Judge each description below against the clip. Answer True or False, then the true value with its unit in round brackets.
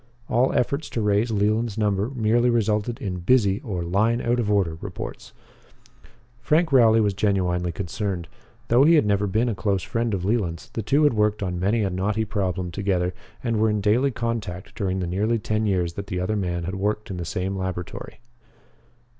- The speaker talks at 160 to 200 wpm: True (190 wpm)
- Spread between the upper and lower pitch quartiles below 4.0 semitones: True (3.5 semitones)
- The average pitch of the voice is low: True (105 Hz)